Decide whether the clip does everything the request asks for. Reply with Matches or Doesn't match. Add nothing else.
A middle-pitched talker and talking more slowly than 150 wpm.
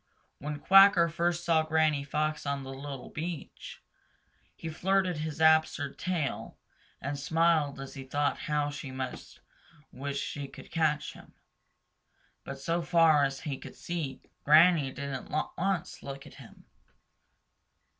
Matches